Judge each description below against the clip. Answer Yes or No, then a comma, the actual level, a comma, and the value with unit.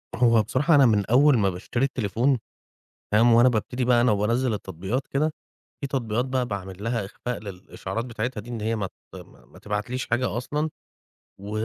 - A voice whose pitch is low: Yes, low, 115 Hz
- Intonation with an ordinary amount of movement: Yes, average, 3.5 semitones